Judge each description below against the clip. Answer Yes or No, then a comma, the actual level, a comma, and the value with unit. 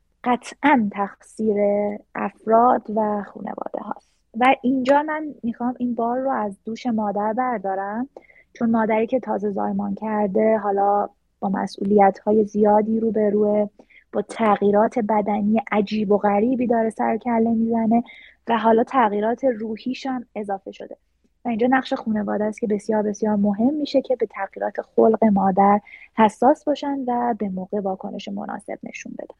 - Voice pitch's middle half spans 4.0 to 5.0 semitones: No, average, 2.9 semitones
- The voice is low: No, high, 220 Hz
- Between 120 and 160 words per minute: Yes, average, 145 wpm